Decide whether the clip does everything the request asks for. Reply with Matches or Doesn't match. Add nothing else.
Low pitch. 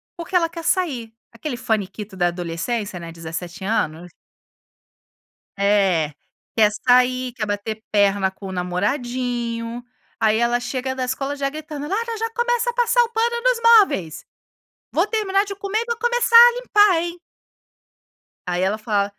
Doesn't match